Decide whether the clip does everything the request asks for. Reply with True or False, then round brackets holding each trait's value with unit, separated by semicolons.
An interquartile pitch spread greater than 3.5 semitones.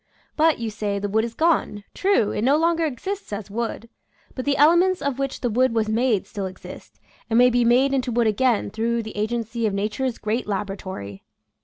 True (4.1 semitones)